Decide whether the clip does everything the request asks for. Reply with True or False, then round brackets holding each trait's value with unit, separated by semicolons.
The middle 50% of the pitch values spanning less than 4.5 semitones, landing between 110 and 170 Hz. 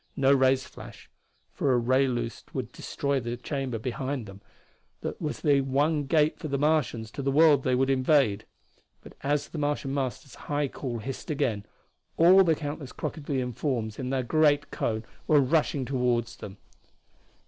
True (2.8 semitones; 135 Hz)